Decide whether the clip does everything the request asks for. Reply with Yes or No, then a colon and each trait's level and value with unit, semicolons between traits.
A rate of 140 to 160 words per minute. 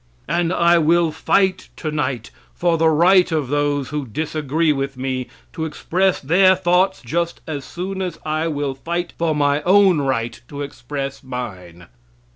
Yes: average, 155 wpm